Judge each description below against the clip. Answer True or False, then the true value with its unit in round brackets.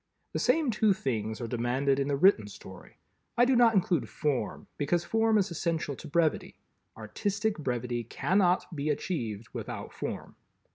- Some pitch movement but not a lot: False (8.4 semitones)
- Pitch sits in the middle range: True (155 Hz)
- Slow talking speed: False (155 wpm)